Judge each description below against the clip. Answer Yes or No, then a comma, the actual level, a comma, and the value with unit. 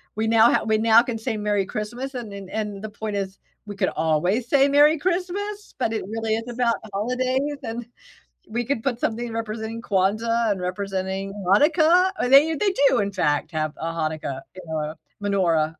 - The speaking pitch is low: No, high, 220 Hz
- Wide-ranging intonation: No, average, 4.3 semitones